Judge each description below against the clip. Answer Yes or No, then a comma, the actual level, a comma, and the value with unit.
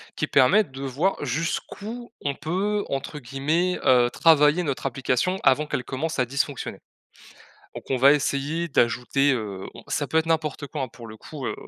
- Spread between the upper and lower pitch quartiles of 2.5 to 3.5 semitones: No, average, 3.9 semitones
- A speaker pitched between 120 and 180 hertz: Yes, medium, 140 Hz